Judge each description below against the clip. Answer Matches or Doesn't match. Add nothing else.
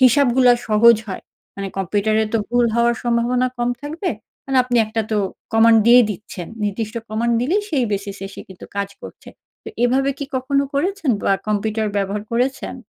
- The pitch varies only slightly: Doesn't match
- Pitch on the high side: Matches